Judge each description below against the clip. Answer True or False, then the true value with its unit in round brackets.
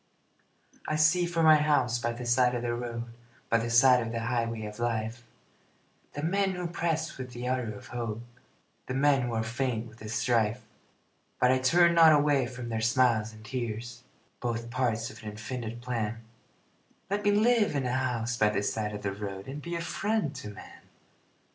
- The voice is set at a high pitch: False (120 Hz)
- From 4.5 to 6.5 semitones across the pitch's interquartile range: False (4.0 semitones)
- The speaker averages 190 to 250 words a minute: True (195 wpm)